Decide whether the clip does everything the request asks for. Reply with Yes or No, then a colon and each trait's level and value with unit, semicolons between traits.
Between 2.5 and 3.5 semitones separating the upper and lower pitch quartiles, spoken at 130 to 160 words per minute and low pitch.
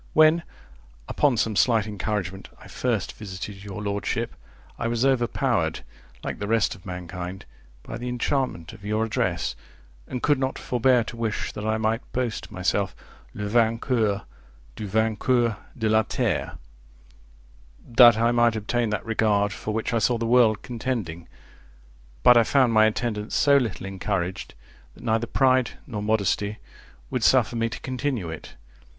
Yes: average, 2.9 semitones; average, 155 wpm; low, 110 Hz